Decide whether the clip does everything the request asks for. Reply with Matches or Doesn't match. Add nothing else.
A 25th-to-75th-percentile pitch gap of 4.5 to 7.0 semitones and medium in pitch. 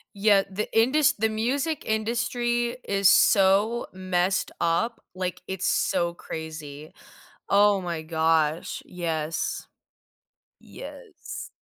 Doesn't match